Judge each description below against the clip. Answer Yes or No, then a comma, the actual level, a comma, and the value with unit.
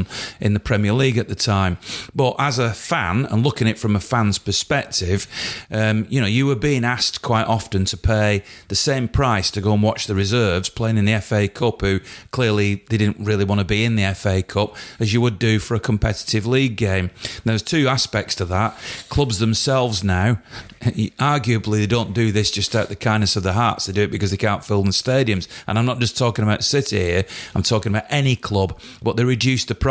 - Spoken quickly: Yes, fast, 230 wpm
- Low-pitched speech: Yes, low, 110 Hz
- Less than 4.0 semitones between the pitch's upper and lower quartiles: Yes, average, 2.8 semitones